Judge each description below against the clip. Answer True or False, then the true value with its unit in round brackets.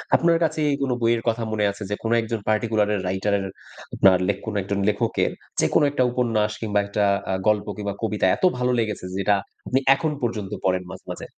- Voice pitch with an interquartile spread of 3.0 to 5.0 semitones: False (2.4 semitones)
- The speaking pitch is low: True (105 Hz)